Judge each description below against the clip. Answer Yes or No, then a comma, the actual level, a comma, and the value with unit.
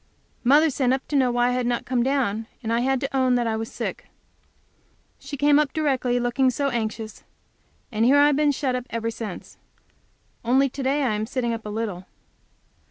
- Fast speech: Yes, fast, 210 wpm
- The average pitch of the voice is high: Yes, very high, 250 Hz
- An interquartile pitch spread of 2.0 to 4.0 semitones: Yes, average, 3.0 semitones